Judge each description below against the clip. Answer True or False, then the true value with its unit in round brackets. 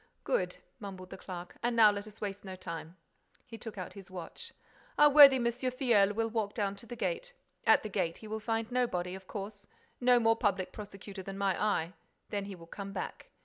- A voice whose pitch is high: True (205 Hz)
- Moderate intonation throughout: True (3.4 semitones)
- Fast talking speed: True (210 wpm)